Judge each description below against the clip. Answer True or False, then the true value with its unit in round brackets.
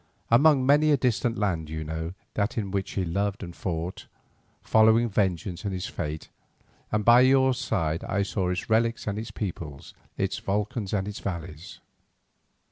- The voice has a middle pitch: False (100 Hz)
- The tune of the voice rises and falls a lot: False (4.7 semitones)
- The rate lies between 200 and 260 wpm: False (165 wpm)